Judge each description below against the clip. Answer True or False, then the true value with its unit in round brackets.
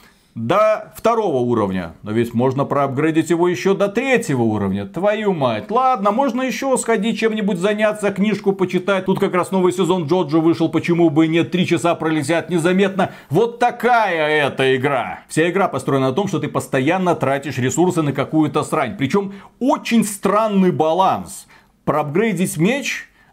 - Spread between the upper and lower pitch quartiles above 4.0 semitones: True (5.4 semitones)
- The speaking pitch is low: False (180 Hz)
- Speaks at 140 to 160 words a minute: True (155 wpm)